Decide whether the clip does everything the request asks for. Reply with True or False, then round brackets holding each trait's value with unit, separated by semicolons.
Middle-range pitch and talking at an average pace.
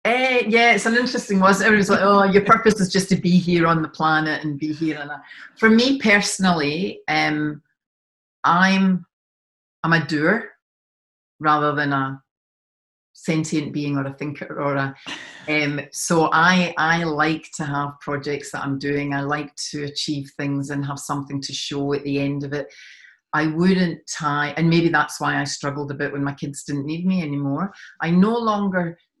True (155 Hz; 185 wpm)